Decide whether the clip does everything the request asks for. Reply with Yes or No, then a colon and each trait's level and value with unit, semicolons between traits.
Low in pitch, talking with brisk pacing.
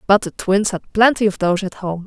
No: high, 195 Hz; fast, 260 wpm